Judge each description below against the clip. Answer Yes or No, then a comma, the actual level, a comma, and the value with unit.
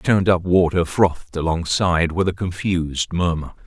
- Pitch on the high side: No, very low, 85 Hz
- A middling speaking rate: Yes, average, 165 wpm